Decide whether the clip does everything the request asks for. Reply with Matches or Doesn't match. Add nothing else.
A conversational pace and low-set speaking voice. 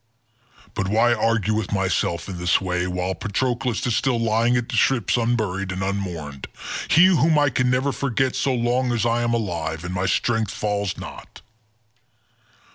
Matches